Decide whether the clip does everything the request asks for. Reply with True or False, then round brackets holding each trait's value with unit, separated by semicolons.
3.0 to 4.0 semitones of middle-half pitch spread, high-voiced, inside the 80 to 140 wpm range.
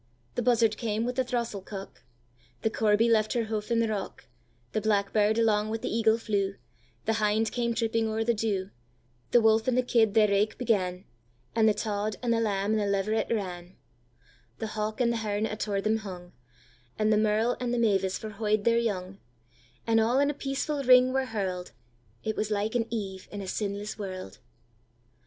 False (3.3 semitones; 210 Hz; 170 wpm)